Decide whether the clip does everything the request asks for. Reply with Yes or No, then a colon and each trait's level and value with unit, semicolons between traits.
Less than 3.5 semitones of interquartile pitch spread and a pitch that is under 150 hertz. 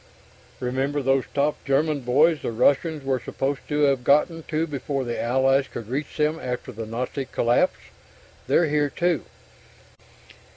Yes: average, 2.9 semitones; medium, 140 Hz